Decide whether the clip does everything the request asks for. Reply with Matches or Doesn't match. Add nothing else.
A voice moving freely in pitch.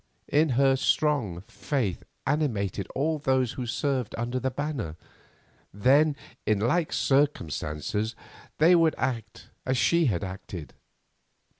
Matches